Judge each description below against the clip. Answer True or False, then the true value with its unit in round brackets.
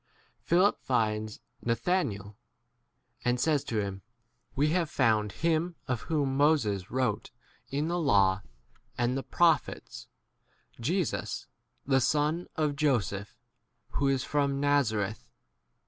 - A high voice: False (135 Hz)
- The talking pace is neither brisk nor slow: False (115 wpm)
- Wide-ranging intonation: True (6.0 semitones)